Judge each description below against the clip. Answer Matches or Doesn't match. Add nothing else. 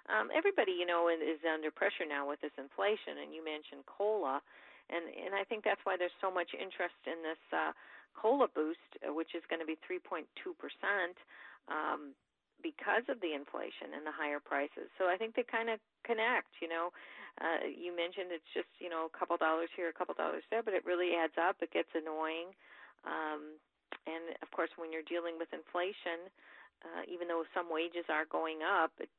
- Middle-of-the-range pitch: Matches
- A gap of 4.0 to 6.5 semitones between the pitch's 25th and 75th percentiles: Doesn't match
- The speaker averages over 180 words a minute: Matches